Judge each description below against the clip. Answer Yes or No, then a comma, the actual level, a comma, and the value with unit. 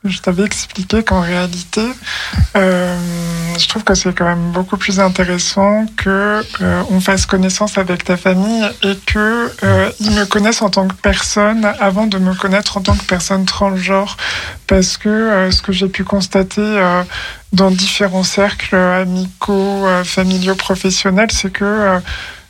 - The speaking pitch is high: Yes, high, 195 Hz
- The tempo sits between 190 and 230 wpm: No, average, 165 wpm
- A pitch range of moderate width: No, narrow, 1.8 semitones